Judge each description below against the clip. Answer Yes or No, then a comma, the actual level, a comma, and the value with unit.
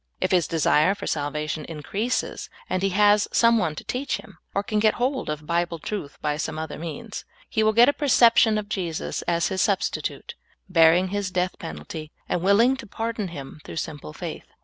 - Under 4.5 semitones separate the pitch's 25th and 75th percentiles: No, average, 5.2 semitones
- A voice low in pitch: No, medium, 185 Hz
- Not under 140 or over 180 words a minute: No, average, 195 wpm